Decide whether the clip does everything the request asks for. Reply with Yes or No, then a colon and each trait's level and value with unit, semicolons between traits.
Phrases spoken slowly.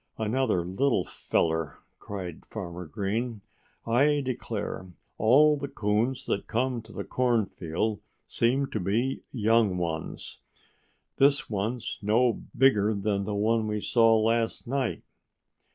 Yes: slow, 120 wpm